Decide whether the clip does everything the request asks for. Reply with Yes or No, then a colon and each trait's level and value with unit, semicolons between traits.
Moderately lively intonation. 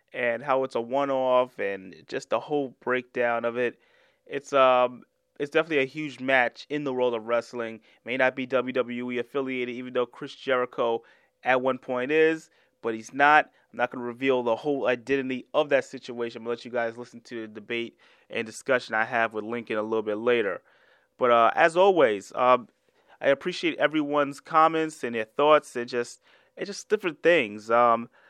Yes: average, 3.1 semitones